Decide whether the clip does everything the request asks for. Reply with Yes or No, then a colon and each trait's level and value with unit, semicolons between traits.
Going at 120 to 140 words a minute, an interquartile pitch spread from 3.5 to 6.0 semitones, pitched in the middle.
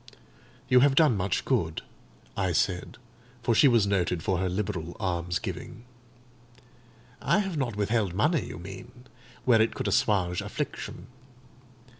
No: slow, 135 wpm; average, 5.3 semitones; low, 105 Hz